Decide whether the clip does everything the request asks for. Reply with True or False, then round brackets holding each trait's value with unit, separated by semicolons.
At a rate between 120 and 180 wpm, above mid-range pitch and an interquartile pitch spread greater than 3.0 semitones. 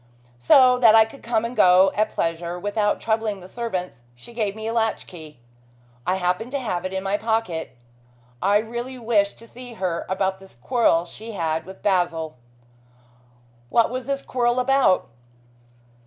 True (170 wpm; 210 Hz; 4.4 semitones)